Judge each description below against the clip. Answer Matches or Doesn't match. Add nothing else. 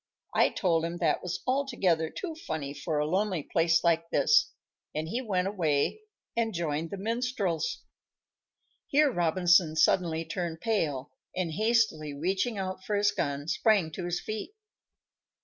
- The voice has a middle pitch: Matches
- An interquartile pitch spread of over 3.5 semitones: Matches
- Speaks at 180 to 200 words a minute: Doesn't match